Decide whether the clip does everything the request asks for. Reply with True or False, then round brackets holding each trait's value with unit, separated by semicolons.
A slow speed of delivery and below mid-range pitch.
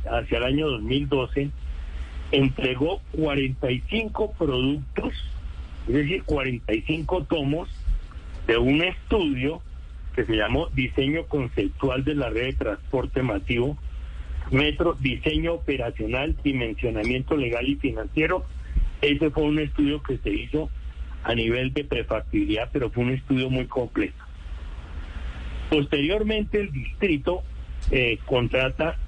True (110 wpm; 130 Hz)